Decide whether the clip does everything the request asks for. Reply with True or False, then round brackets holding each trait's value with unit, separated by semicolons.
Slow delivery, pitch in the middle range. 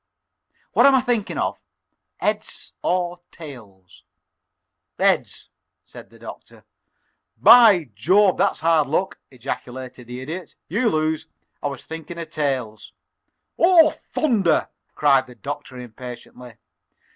True (115 wpm; 155 Hz)